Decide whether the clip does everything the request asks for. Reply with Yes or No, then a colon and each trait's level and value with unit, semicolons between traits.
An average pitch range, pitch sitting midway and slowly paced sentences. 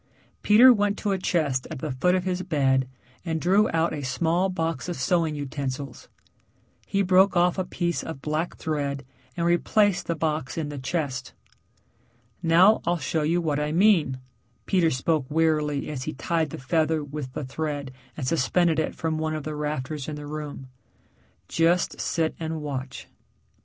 No: average, 3.2 semitones; medium, 160 Hz; average, 175 wpm